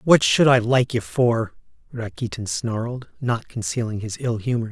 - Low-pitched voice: Yes, low, 120 Hz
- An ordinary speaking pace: Yes, average, 165 wpm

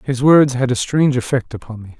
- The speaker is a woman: No, male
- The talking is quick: Yes, fast, 240 wpm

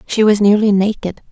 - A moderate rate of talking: Yes, average, 180 wpm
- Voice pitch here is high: Yes, high, 205 Hz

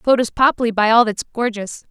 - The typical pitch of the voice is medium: No, high, 230 Hz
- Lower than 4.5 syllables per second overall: No, 4.9 syllables/s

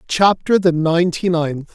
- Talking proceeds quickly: No, slow, 135 wpm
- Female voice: No, male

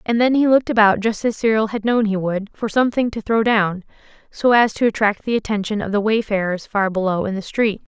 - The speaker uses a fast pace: Yes, fast, 235 wpm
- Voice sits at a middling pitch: No, high, 215 Hz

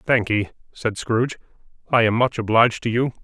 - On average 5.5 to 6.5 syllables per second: Yes, 5.8 syllables/s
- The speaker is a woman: No, male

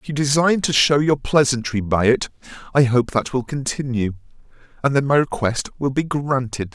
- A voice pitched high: No, low, 130 Hz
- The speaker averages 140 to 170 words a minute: No, average, 185 wpm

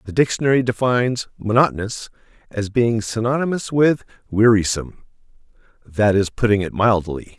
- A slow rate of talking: Yes, slow, 115 wpm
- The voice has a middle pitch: No, low, 115 Hz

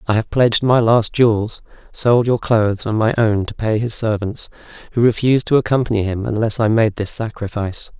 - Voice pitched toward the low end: Yes, low, 110 Hz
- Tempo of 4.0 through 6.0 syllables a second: Yes, 5.6 syllables/s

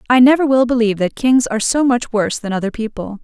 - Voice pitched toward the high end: Yes, high, 235 Hz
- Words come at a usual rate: No, fast, 240 wpm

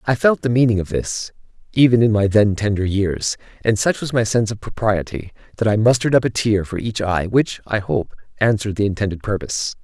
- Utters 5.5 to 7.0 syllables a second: Yes, 5.9 syllables/s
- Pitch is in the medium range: No, low, 110 Hz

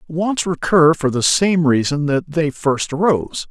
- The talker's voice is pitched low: No, medium, 155 Hz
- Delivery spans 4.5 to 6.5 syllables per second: No, 4.2 syllables/s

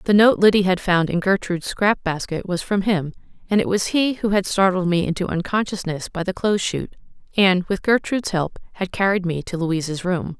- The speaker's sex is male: No, female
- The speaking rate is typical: No, fast, 210 wpm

